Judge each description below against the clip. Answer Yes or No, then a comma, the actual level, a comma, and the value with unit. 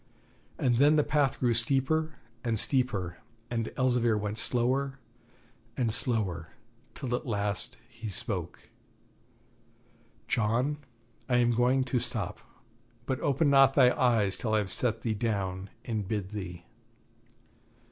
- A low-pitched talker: Yes, low, 120 Hz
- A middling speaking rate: No, slow, 130 wpm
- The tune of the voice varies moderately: Yes, average, 3.8 semitones